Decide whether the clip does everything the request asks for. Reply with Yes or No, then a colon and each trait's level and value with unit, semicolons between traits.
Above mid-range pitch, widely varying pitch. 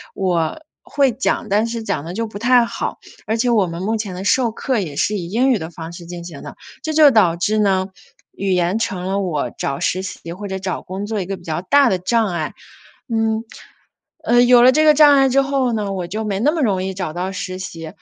No: high, 200 Hz; average, 4.6 semitones